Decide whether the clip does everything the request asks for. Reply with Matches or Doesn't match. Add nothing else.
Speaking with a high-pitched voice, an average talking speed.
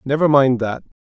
Doesn't match